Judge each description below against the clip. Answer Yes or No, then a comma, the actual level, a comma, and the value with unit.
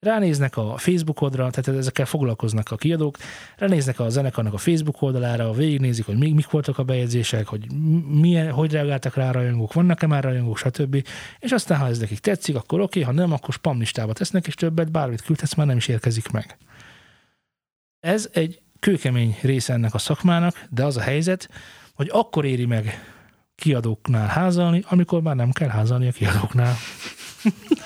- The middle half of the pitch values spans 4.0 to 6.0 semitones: Yes, average, 5.2 semitones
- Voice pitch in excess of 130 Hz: Yes, medium, 140 Hz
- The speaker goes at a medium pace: No, fast, 170 wpm